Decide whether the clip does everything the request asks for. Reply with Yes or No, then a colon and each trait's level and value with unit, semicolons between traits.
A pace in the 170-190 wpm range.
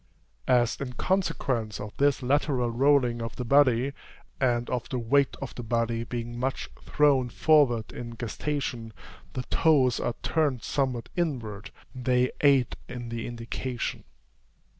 No: average, 140 wpm